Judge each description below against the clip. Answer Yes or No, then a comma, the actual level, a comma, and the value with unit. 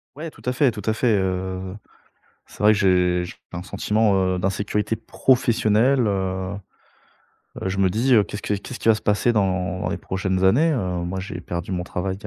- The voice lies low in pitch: Yes, low, 100 Hz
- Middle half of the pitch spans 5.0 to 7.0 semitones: No, average, 3.0 semitones